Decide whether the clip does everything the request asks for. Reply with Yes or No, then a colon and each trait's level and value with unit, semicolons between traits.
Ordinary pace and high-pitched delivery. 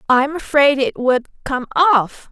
Yes: average, 155 wpm; very high, 270 Hz